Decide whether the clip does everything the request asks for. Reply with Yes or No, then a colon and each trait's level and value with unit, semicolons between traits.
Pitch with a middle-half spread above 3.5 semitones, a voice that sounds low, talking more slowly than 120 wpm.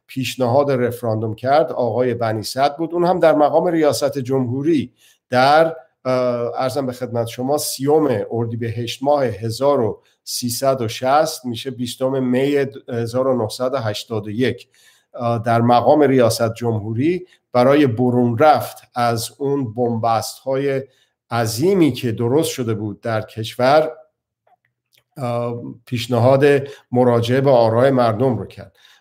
No: average, 3.0 semitones; low, 125 Hz; average, 110 wpm